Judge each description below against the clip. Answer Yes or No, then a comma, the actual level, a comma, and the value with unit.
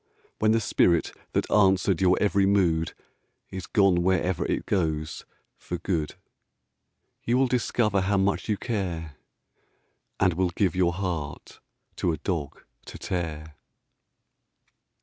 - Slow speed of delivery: Yes, slow, 130 wpm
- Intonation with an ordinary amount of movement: Yes, average, 3.2 semitones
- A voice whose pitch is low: Yes, very low, 95 Hz